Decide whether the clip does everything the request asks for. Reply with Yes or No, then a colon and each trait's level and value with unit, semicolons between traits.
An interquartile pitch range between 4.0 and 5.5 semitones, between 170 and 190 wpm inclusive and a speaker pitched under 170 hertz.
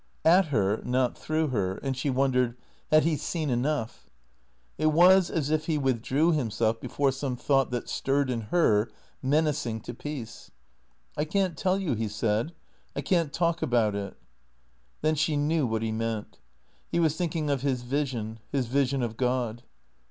Yes: average, 5.1 semitones; average, 175 wpm; low, 135 Hz